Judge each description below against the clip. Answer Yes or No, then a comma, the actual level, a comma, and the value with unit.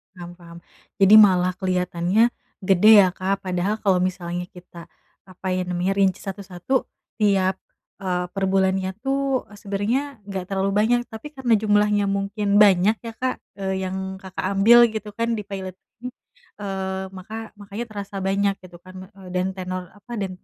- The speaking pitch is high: Yes, high, 195 Hz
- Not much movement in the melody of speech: Yes, narrow, 2.0 semitones